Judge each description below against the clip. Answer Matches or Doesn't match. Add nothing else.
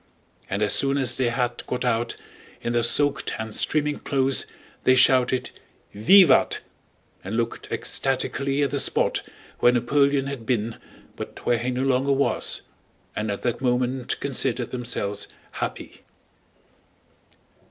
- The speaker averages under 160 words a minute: Matches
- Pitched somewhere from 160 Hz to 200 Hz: Doesn't match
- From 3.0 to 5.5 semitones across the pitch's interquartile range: Doesn't match